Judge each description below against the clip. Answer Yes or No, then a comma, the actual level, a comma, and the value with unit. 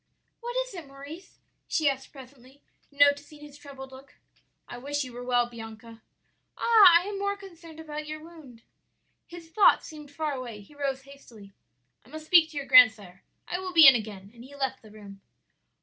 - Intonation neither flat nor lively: Yes, average, 4.5 semitones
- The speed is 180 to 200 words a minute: Yes, average, 185 wpm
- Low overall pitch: No, very high, 280 Hz